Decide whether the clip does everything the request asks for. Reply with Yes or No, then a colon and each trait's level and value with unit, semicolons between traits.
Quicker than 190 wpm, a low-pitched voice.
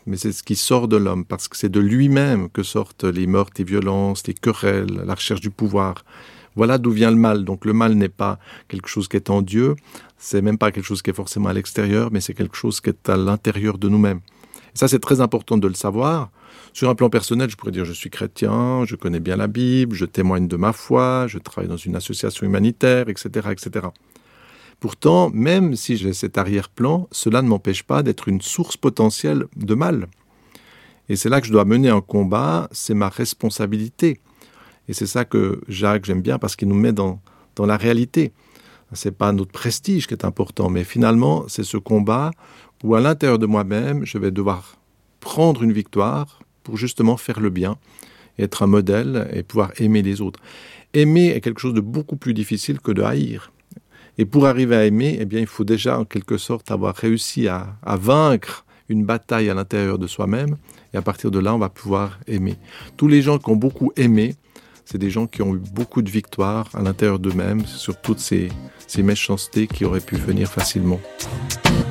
Yes: average, 210 wpm; low, 105 Hz